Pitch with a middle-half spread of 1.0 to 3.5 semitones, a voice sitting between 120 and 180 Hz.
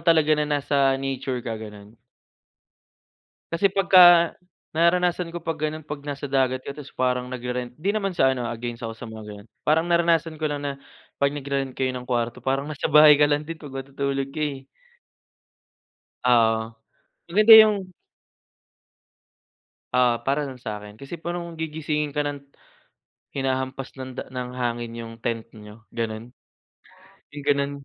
No: average, 4.0 semitones; low, 135 Hz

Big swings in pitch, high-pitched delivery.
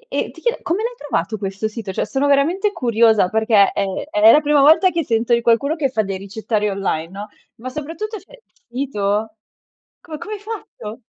Yes: wide, 6.7 semitones; high, 235 Hz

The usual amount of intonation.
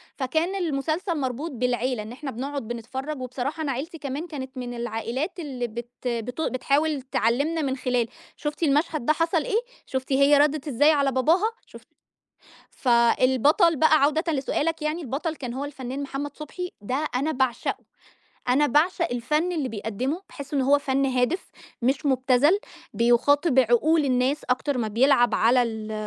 Yes: average, 3.6 semitones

